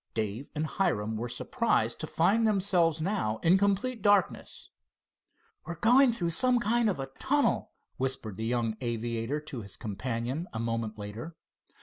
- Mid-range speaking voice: Yes, medium, 150 Hz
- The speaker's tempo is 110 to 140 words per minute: No, average, 150 wpm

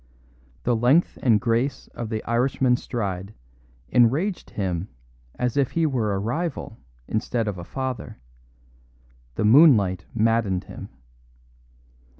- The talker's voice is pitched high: No, low, 115 Hz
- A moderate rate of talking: No, slow, 120 wpm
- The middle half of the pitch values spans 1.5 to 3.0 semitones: No, average, 3.9 semitones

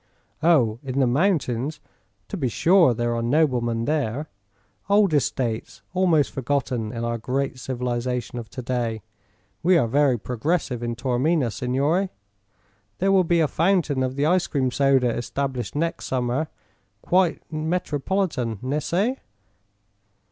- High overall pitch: No, low, 135 Hz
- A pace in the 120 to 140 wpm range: Yes, slow, 135 wpm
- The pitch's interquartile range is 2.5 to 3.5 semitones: No, average, 5.0 semitones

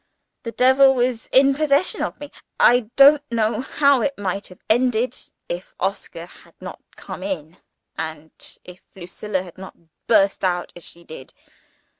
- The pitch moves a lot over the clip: Yes, wide, 6.7 semitones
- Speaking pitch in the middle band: No, high, 225 Hz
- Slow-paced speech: No, average, 155 wpm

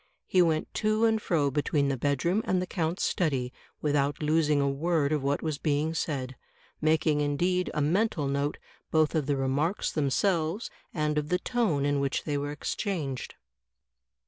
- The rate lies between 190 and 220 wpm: No, average, 175 wpm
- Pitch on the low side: No, medium, 150 Hz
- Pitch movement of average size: Yes, average, 3.3 semitones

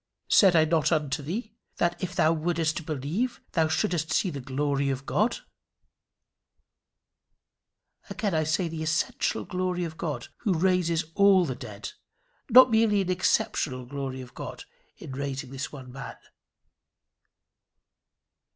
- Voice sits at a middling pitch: Yes, medium, 160 Hz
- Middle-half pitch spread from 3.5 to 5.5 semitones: Yes, average, 4.5 semitones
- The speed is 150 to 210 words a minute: No, average, 140 wpm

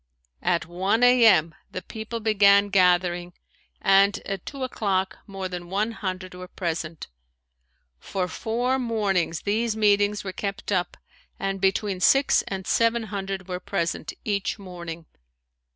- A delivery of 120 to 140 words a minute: Yes, slow, 135 wpm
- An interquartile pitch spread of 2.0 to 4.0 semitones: Yes, average, 2.9 semitones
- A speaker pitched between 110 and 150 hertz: No, high, 195 Hz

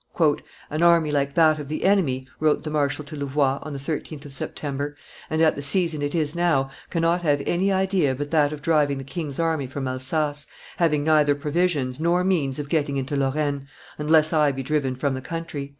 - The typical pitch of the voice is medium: Yes, medium, 150 Hz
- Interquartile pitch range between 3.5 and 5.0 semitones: No, narrow, 2.5 semitones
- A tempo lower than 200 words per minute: No, fast, 205 wpm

